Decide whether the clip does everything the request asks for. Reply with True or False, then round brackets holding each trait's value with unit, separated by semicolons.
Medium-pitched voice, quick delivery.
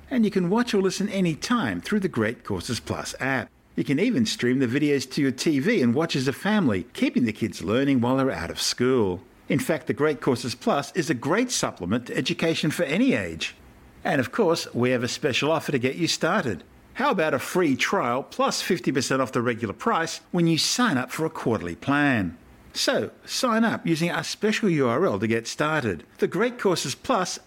True (155 Hz; 210 wpm)